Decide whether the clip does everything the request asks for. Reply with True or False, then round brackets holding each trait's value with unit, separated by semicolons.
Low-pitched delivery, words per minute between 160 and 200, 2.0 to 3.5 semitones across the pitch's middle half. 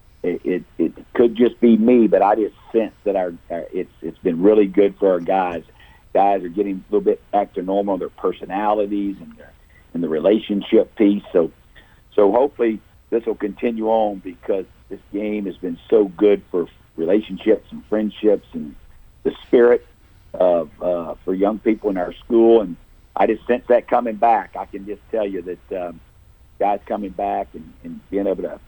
True (105 Hz; 185 wpm; 2.6 semitones)